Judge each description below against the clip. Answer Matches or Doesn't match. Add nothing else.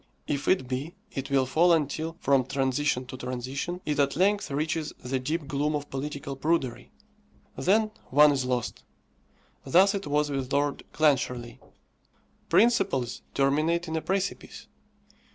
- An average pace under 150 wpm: Matches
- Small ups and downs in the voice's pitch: Doesn't match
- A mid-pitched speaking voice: Matches